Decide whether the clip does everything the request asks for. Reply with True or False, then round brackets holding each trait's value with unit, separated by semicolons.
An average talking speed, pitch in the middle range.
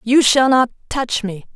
False (195 wpm; 245 Hz)